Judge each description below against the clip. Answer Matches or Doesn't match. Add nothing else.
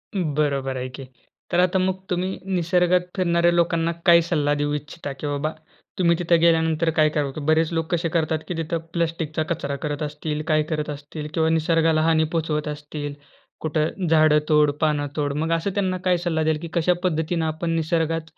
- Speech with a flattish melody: Matches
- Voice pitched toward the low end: Doesn't match